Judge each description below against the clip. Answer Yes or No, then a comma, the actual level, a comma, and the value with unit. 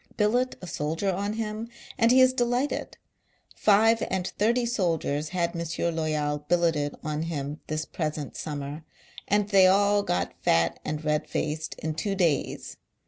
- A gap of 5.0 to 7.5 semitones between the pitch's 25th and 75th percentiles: Yes, wide, 5.4 semitones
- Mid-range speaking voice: Yes, medium, 170 Hz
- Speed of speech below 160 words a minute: Yes, average, 150 wpm